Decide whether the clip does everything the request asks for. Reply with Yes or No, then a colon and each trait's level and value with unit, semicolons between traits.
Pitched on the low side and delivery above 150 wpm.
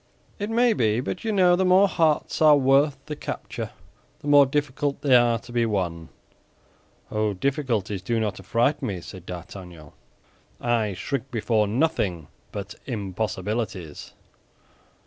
No: low, 120 Hz; average, 140 wpm